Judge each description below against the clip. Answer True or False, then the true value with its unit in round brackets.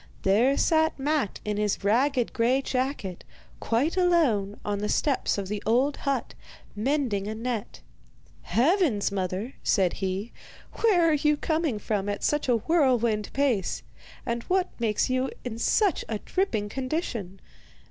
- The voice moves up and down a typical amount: False (6.0 semitones)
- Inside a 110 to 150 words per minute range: True (145 wpm)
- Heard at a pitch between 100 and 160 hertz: False (240 Hz)